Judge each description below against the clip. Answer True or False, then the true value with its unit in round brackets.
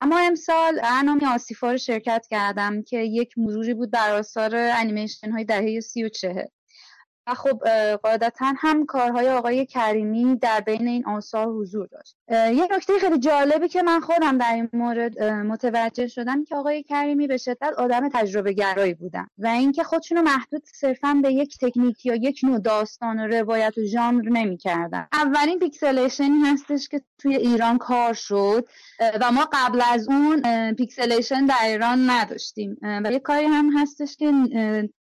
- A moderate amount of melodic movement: True (4.2 semitones)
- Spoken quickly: True (160 wpm)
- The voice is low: False (245 Hz)